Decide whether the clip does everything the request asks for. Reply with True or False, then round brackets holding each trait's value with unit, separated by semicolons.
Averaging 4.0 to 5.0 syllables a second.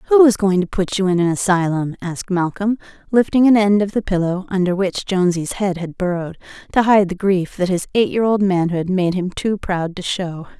False (5.4 syllables/s)